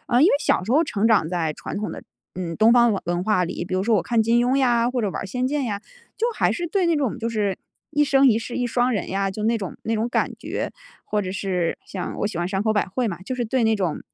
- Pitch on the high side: Yes, high, 220 Hz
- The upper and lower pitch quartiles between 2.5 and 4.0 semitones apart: No, average, 4.4 semitones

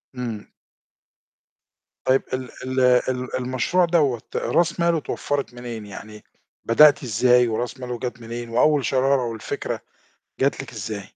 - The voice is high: No, low, 125 Hz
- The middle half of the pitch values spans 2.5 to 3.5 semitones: Yes, average, 2.9 semitones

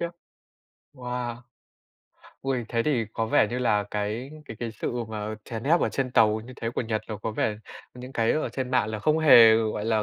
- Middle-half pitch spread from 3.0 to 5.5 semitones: No, narrow, 2.6 semitones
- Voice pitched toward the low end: Yes, low, 115 Hz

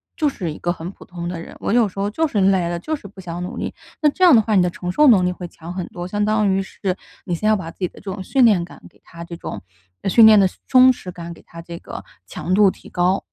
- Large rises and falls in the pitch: No, average, 3.5 semitones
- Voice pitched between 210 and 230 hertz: No, high, 190 Hz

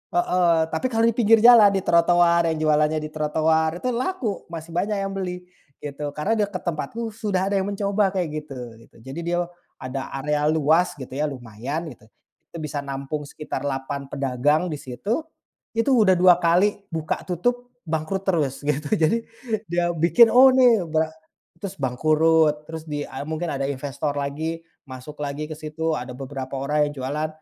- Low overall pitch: No, medium, 160 Hz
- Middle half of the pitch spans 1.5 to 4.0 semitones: No, average, 4.4 semitones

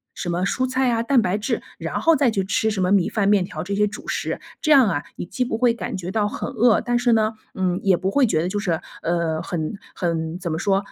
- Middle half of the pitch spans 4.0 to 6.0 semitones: Yes, average, 4.6 semitones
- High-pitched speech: Yes, high, 200 Hz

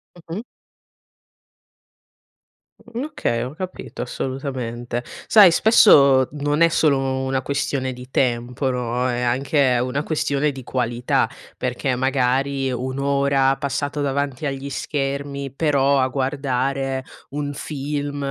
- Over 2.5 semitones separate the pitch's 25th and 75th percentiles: No, narrow, 1.9 semitones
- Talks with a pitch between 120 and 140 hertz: Yes, low, 135 Hz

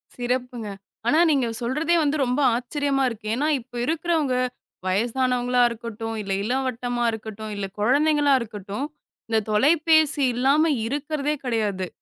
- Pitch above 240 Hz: Yes, very high, 250 Hz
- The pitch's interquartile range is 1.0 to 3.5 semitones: No, average, 4.3 semitones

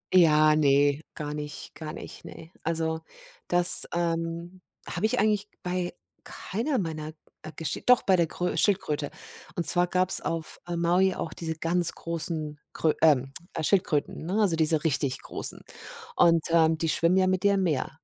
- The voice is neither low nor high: Yes, medium, 165 Hz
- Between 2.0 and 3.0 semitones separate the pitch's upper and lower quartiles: Yes, narrow, 2.6 semitones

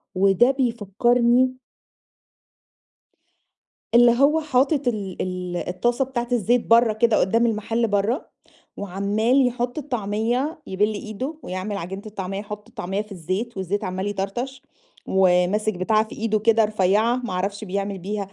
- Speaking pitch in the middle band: No, high, 215 Hz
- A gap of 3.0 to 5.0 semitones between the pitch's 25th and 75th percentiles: Yes, average, 3.6 semitones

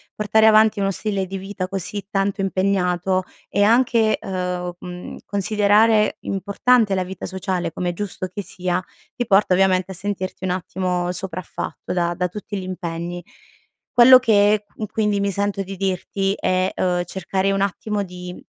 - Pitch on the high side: Yes, high, 195 Hz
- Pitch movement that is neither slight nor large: No, narrow, 2.1 semitones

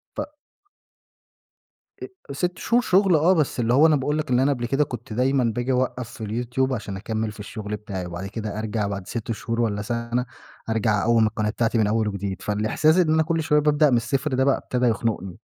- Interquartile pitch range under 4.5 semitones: No, average, 5.0 semitones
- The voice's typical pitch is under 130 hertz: Yes, low, 120 Hz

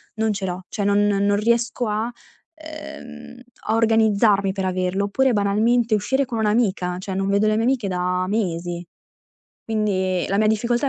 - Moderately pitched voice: No, high, 210 Hz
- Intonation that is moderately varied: Yes, average, 3.3 semitones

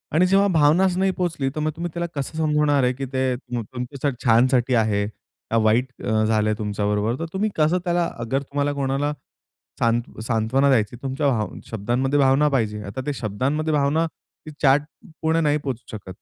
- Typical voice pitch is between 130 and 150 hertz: Yes, low, 135 Hz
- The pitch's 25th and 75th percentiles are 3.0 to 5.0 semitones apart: Yes, average, 4.7 semitones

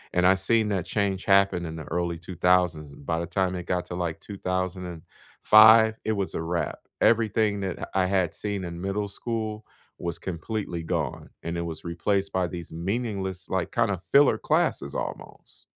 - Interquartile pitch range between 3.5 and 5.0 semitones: No, average, 3.0 semitones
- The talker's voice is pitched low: Yes, very low, 95 Hz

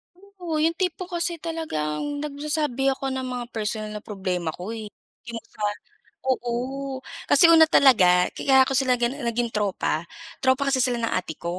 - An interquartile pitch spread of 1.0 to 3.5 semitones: No, average, 5.3 semitones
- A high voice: Yes, very high, 260 Hz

